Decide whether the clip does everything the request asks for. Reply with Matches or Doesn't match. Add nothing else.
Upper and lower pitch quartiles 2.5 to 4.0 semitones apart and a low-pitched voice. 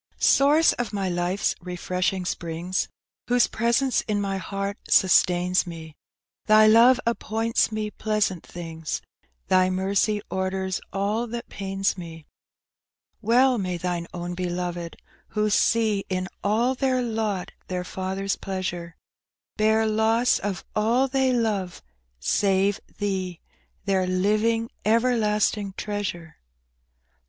Doesn't match